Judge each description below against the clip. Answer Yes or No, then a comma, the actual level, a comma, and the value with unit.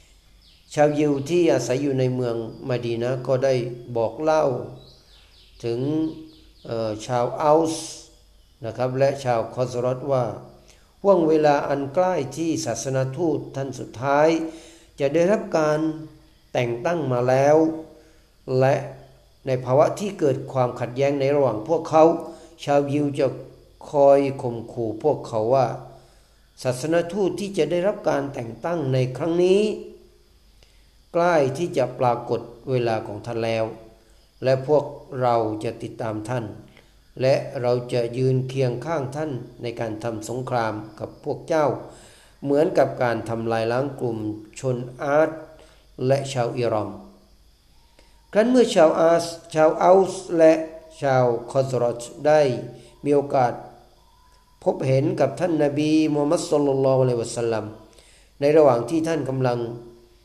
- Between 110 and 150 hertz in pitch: Yes, low, 130 Hz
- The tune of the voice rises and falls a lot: No, average, 4.9 semitones